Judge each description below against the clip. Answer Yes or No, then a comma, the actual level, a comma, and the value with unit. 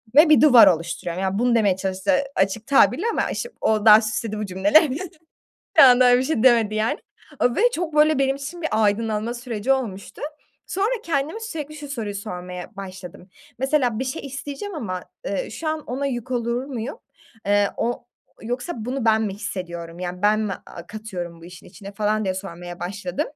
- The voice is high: Yes, high, 225 Hz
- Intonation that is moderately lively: No, wide, 5.8 semitones